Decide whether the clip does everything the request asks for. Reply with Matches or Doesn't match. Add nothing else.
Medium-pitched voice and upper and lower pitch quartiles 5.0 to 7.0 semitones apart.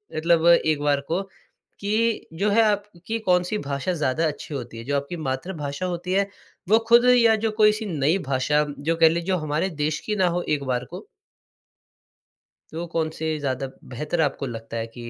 Matches